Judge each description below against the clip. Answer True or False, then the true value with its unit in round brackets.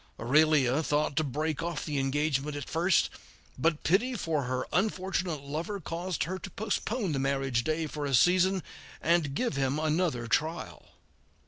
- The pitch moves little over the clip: False (4.1 semitones)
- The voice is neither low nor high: True (155 Hz)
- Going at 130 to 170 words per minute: True (155 wpm)